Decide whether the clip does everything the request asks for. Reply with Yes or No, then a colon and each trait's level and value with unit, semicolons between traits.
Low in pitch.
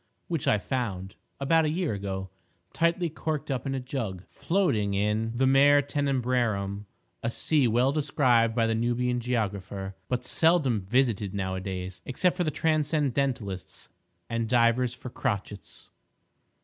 Yes: low, 120 Hz